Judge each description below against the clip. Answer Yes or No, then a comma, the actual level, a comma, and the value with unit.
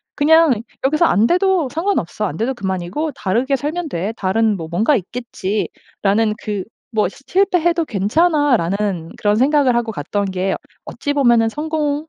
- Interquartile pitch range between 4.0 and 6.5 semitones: No, wide, 7.1 semitones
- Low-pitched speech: No, high, 235 Hz